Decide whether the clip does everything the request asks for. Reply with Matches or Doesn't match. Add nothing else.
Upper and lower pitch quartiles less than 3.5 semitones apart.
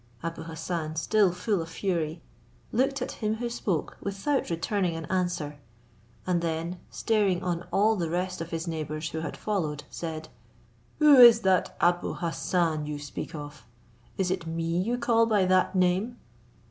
Doesn't match